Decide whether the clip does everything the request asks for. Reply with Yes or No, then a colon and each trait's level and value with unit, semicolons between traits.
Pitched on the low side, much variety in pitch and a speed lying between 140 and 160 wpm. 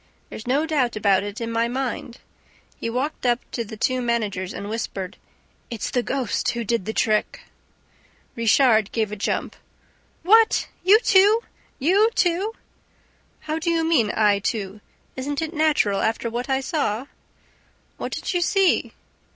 No: high, 245 Hz; wide, 6.4 semitones; average, 155 wpm